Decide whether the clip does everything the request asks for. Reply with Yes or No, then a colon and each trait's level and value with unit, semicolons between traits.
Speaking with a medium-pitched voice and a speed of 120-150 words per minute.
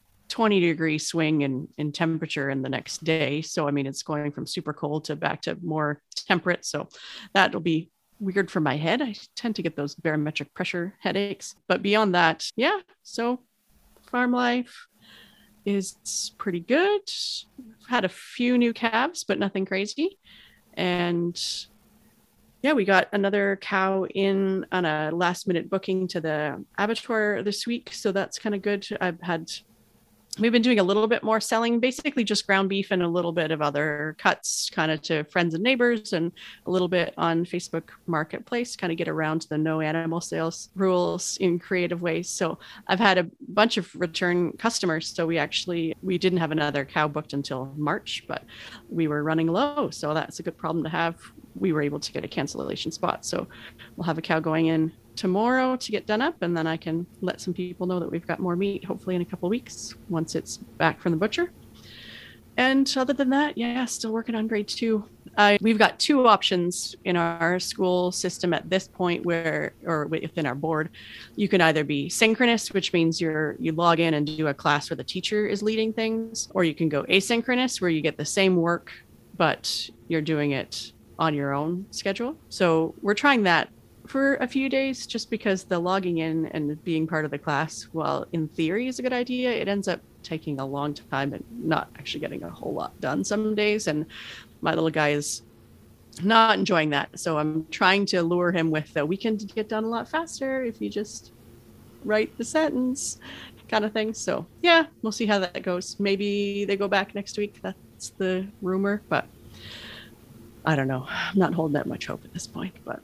No: medium, 180 Hz; average, 195 wpm